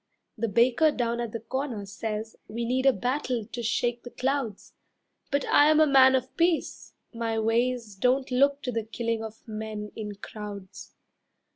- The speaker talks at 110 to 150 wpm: No, average, 170 wpm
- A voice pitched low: No, high, 235 Hz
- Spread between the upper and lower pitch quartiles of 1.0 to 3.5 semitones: Yes, average, 3.0 semitones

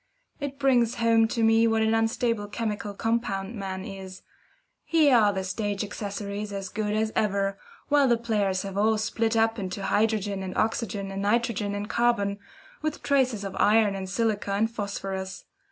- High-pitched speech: Yes, high, 210 Hz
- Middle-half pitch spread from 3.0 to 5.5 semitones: No, narrow, 2.4 semitones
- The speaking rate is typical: Yes, average, 170 wpm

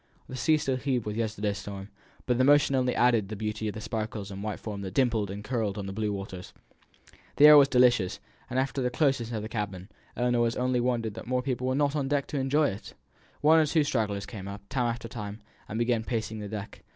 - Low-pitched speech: Yes, low, 115 Hz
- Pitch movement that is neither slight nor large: Yes, average, 3.7 semitones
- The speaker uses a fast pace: Yes, fast, 235 wpm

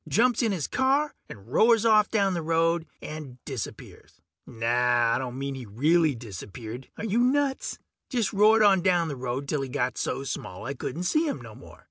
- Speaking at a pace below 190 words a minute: No, average, 195 wpm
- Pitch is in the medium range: Yes, medium, 160 Hz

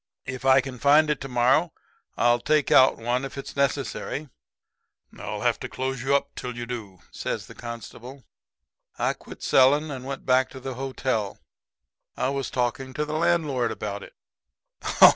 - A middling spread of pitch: No, narrow, 2.3 semitones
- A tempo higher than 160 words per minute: Yes, average, 170 wpm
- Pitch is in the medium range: No, low, 130 Hz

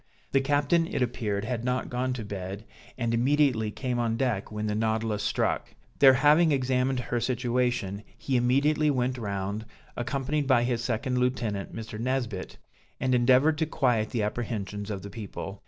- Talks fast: No, average, 165 wpm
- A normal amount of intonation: Yes, average, 3.3 semitones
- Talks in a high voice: No, low, 120 Hz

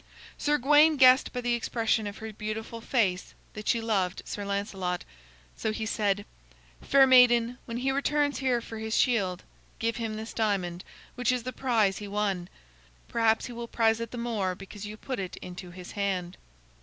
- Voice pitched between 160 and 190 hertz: No, high, 220 Hz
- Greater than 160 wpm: Yes, average, 180 wpm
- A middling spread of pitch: Yes, average, 3.4 semitones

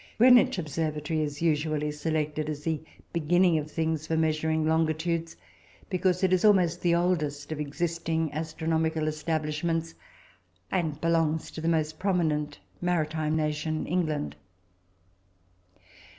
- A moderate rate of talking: No, slow, 120 wpm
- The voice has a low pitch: No, medium, 160 Hz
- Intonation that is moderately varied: No, narrow, 1.7 semitones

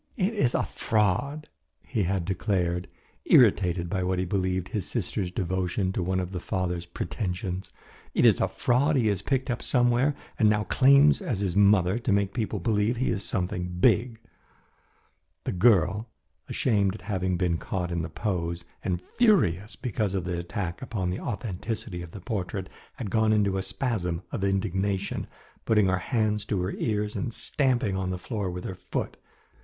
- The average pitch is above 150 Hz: No, low, 100 Hz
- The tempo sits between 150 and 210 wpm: Yes, average, 175 wpm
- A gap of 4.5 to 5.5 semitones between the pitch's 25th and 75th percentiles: No, average, 3.6 semitones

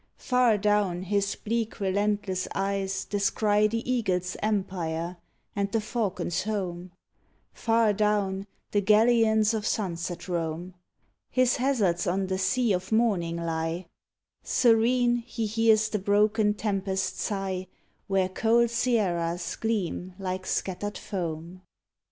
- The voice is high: Yes, high, 200 Hz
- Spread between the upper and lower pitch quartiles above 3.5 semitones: No, average, 3.1 semitones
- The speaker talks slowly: Yes, slow, 120 wpm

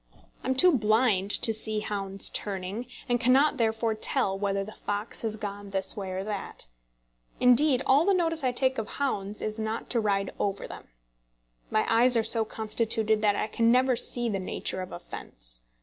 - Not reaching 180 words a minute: No, average, 190 wpm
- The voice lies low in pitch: No, high, 220 Hz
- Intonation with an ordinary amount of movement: Yes, average, 3.4 semitones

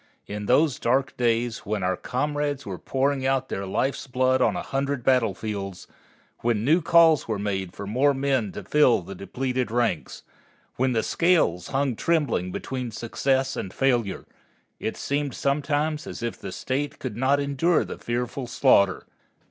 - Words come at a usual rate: Yes, average, 160 wpm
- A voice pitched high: No, low, 130 Hz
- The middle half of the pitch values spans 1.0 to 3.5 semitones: No, average, 4.1 semitones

